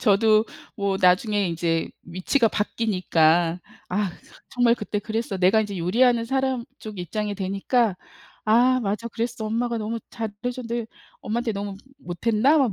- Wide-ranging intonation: No, average, 3.5 semitones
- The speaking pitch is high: Yes, high, 215 Hz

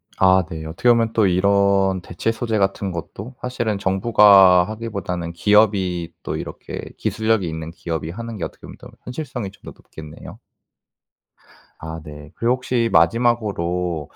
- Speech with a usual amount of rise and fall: Yes, average, 4.7 semitones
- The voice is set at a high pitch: No, very low, 95 Hz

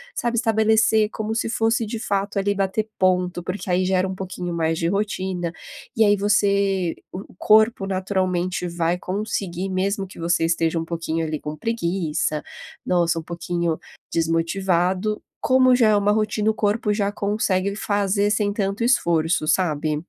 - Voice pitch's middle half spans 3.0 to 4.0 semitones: Yes, average, 3.4 semitones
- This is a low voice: No, high, 190 Hz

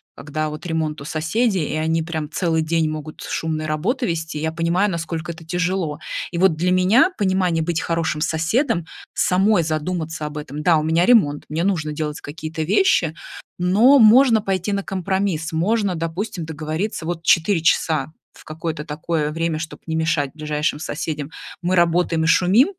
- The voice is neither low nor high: Yes, medium, 165 Hz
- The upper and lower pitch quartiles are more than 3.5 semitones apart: No, average, 2.9 semitones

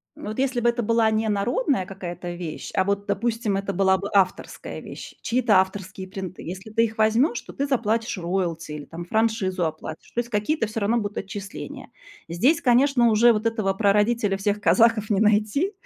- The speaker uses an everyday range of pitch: Yes, average, 3.2 semitones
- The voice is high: Yes, high, 210 Hz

